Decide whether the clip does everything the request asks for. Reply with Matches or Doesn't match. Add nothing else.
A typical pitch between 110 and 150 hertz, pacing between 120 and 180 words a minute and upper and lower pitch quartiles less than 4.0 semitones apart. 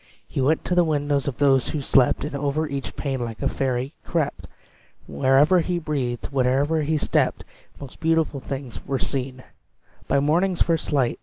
Matches